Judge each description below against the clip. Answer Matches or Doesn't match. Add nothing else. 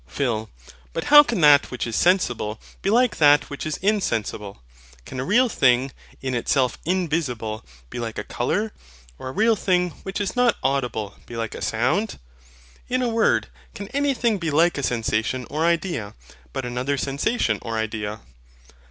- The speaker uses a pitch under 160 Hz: Matches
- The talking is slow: Doesn't match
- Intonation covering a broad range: Matches